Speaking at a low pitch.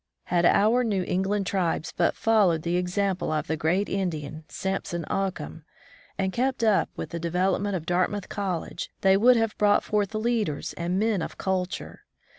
No: high, 190 Hz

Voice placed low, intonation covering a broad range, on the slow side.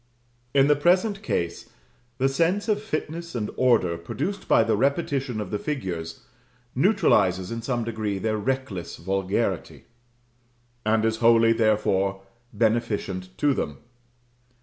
Yes: low, 115 Hz; wide, 6.2 semitones; slow, 125 wpm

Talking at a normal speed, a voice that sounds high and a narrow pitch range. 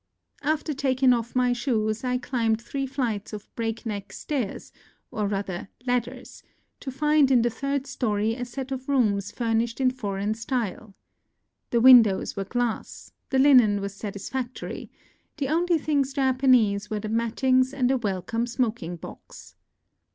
No: average, 150 wpm; high, 245 Hz; average, 3.6 semitones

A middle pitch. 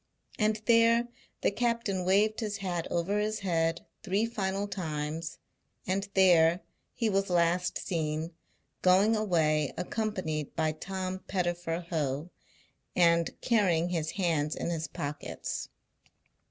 Yes: medium, 180 Hz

